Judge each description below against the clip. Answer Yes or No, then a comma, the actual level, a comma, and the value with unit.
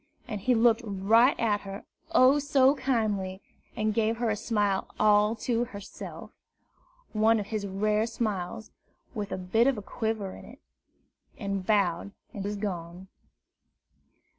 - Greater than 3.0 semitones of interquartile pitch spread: No, narrow, 2.5 semitones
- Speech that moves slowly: No, average, 145 wpm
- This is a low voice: No, high, 215 Hz